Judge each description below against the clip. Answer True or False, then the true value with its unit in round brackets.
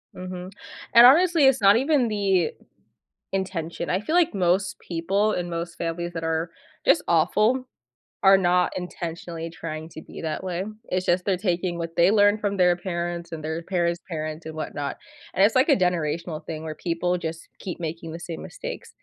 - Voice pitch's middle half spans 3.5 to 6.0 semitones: False (3.0 semitones)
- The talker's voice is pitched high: False (175 Hz)